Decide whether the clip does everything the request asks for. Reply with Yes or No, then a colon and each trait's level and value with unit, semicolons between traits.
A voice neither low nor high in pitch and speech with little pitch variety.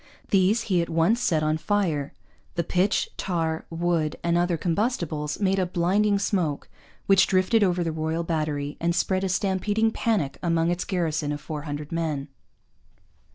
No: medium, 170 Hz; average, 3.3 semitones